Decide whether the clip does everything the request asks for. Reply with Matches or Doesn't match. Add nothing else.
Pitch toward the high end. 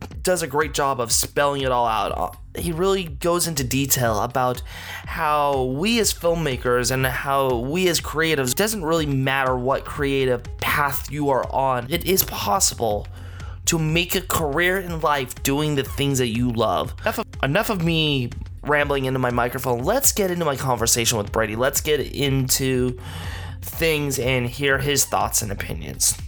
Doesn't match